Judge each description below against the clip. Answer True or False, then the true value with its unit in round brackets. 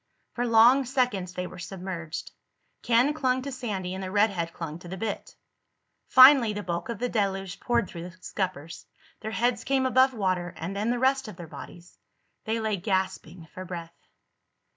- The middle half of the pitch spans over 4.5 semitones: True (5.2 semitones)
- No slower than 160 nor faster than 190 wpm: True (180 wpm)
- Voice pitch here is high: True (200 Hz)